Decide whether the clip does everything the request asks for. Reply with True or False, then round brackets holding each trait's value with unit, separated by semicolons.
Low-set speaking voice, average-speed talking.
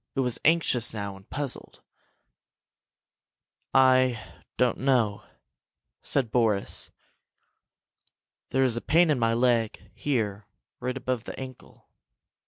False (125 Hz; 110 wpm)